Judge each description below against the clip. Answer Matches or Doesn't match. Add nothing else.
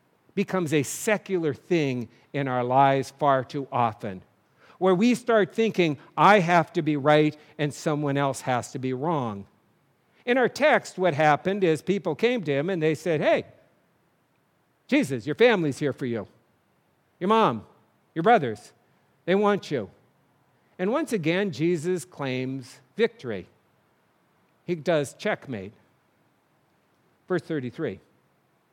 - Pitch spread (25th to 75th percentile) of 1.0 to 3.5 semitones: Doesn't match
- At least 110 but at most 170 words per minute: Matches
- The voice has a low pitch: Doesn't match